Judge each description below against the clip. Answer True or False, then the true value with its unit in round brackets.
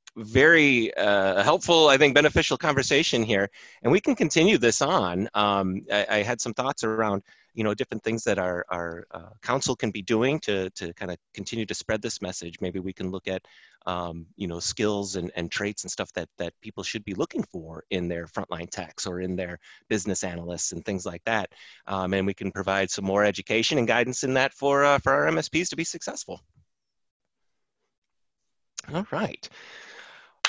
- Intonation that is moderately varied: True (4.5 semitones)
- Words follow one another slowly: False (195 wpm)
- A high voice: False (100 Hz)